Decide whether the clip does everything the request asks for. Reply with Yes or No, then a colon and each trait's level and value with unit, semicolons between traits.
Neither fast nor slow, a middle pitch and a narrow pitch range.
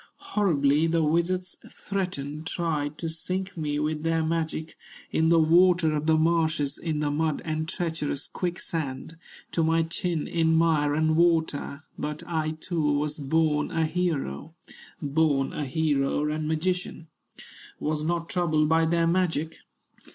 Yes: average, 145 wpm; medium, 160 Hz; narrow, 1.9 semitones